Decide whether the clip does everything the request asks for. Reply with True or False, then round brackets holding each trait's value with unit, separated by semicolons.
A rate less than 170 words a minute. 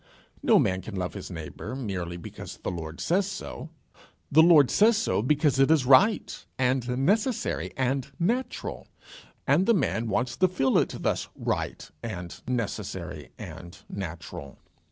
True (150 wpm)